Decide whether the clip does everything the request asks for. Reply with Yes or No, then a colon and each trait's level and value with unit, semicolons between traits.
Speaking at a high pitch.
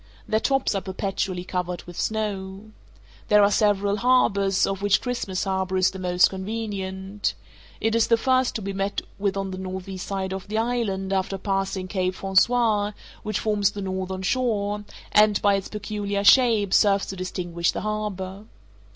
Yes: high, 195 Hz